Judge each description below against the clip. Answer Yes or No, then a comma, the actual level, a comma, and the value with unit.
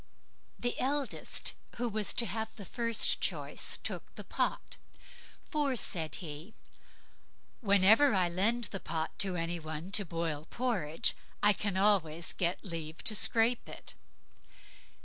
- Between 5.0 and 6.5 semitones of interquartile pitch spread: Yes, wide, 5.5 semitones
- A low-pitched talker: No, high, 195 Hz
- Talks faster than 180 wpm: No, slow, 135 wpm